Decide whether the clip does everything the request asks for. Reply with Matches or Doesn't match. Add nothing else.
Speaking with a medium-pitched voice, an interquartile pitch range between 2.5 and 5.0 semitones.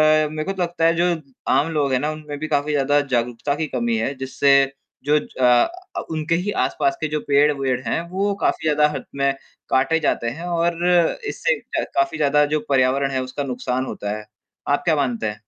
Matches